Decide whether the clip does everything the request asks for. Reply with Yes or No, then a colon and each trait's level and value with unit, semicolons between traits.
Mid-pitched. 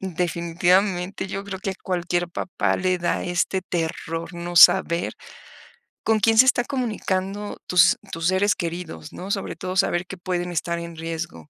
Yes: medium, 180 Hz